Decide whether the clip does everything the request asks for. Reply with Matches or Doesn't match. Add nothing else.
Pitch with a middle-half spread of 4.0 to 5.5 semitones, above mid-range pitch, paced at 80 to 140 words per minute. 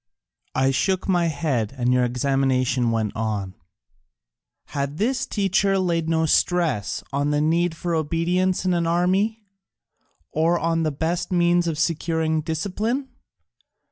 Doesn't match